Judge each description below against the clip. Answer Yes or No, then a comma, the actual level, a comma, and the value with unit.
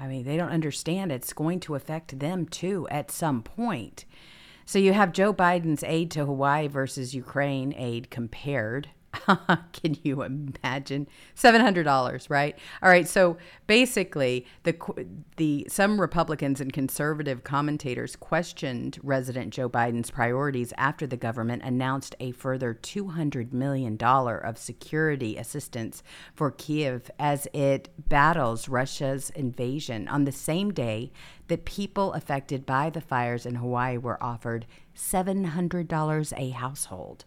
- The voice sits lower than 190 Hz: Yes, medium, 140 Hz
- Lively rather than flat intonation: No, average, 4.4 semitones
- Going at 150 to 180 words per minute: No, average, 140 wpm